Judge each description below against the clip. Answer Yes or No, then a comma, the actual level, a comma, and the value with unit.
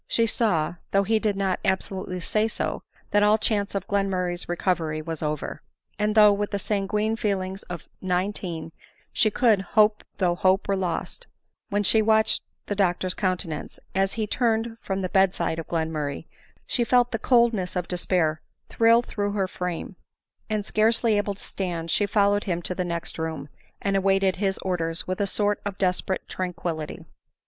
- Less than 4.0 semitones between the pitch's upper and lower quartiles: Yes, average, 2.9 semitones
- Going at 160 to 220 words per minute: Yes, average, 175 wpm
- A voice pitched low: No, high, 195 Hz